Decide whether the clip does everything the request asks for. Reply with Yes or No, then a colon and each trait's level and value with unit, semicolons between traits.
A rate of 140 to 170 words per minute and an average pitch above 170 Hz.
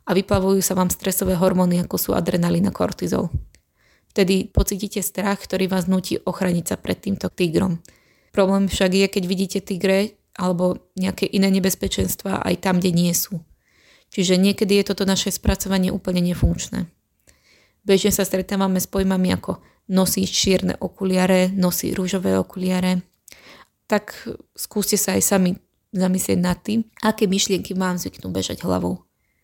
Yes: average, 145 wpm; high, 190 Hz